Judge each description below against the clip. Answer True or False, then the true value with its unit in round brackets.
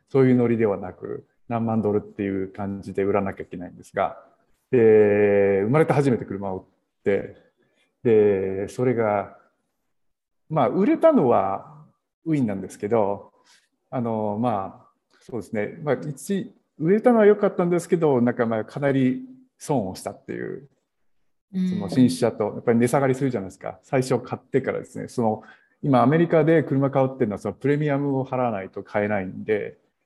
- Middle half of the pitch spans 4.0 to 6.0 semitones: False (6.8 semitones)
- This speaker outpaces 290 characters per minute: True (330 characters per minute)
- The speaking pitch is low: True (125 Hz)